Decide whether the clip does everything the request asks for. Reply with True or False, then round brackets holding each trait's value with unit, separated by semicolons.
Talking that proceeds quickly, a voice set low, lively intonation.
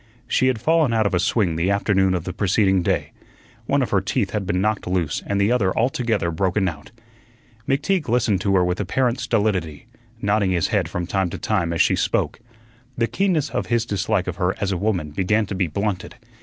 False (210 wpm; 100 Hz; 3.7 semitones)